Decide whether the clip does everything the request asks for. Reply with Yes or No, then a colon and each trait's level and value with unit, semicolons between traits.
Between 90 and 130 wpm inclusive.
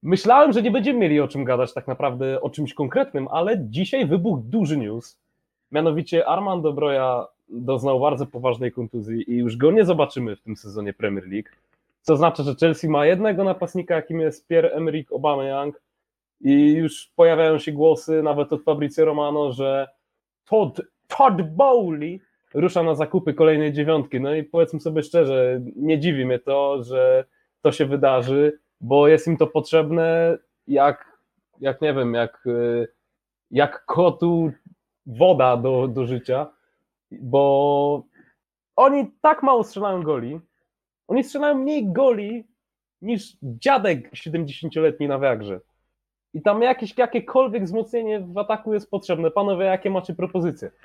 No: average, 145 wpm